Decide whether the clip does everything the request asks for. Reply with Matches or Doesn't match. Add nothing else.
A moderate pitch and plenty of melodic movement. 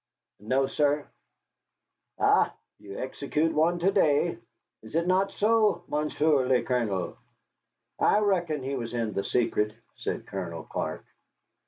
Matches